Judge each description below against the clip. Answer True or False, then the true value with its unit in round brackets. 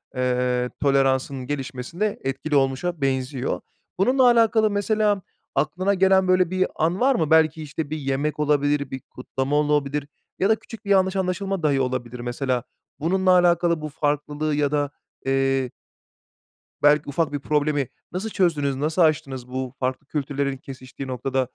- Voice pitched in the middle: True (145 Hz)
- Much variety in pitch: False (4.9 semitones)